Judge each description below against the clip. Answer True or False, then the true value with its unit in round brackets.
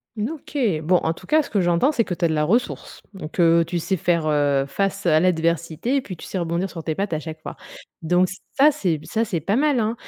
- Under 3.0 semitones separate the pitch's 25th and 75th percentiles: False (4.6 semitones)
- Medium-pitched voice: True (175 Hz)